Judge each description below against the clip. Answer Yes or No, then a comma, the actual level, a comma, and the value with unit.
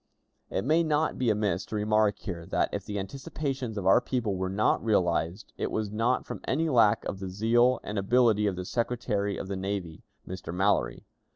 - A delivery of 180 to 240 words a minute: Yes, average, 195 wpm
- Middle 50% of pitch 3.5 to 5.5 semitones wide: Yes, average, 4.0 semitones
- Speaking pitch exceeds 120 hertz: No, low, 105 Hz